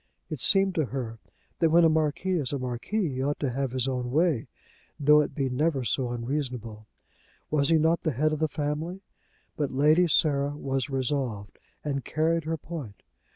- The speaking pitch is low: No, medium, 145 Hz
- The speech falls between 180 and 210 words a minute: Yes, average, 185 wpm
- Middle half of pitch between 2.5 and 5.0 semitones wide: Yes, average, 3.5 semitones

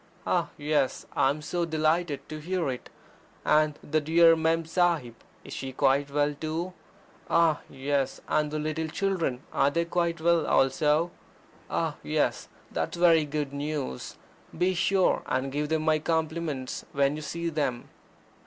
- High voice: No, medium, 155 Hz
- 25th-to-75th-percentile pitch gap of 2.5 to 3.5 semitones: Yes, average, 2.8 semitones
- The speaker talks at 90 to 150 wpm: No, average, 160 wpm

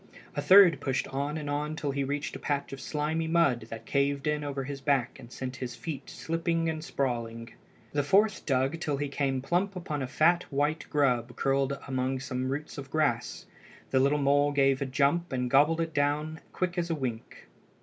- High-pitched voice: No, medium, 140 Hz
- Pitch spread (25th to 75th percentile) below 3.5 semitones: Yes, average, 2.9 semitones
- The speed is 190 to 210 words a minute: Yes, average, 200 wpm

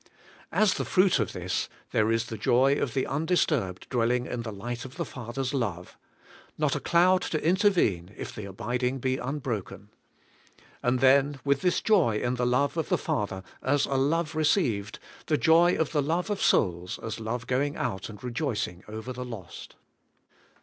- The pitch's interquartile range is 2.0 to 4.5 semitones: No, average, 5.2 semitones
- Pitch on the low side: Yes, low, 125 Hz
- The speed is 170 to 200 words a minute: Yes, average, 180 wpm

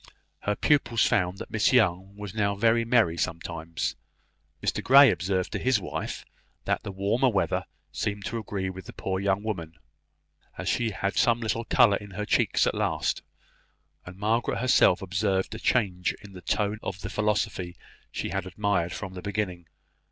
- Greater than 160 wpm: Yes, average, 175 wpm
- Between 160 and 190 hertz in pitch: No, low, 100 Hz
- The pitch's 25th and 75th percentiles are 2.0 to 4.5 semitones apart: Yes, average, 2.9 semitones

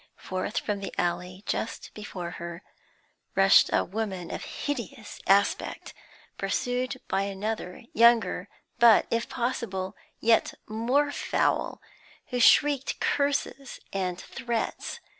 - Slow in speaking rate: Yes, slow, 110 wpm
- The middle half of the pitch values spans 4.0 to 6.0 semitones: Yes, average, 4.4 semitones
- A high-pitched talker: Yes, high, 220 Hz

